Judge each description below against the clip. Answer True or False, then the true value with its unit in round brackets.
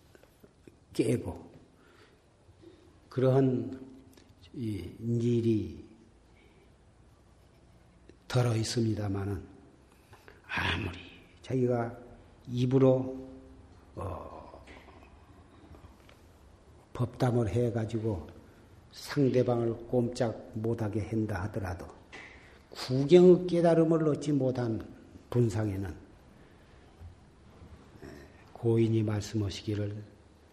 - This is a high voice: False (110 Hz)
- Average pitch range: True (4.9 semitones)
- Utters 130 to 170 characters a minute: True (140 characters per minute)